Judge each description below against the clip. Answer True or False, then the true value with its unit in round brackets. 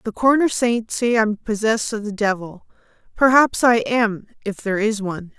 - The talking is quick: False (165 wpm)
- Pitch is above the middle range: True (220 Hz)